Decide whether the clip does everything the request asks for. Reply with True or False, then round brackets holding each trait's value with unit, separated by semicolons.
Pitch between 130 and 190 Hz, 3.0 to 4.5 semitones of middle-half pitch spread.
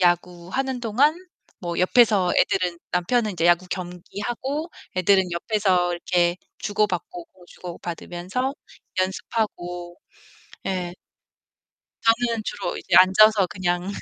True (185 Hz; 3.9 semitones)